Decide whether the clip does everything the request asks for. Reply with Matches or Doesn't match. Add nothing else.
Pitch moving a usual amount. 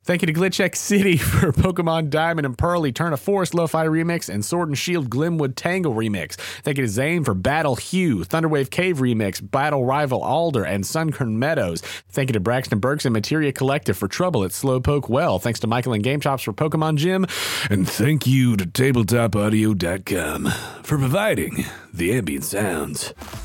Doesn't match